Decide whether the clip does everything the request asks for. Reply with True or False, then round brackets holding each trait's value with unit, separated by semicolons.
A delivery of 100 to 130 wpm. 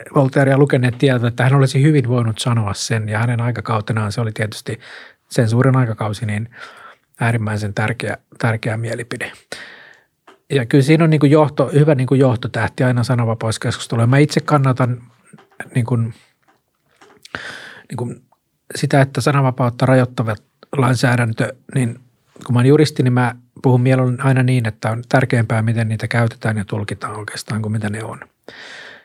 False (155 wpm)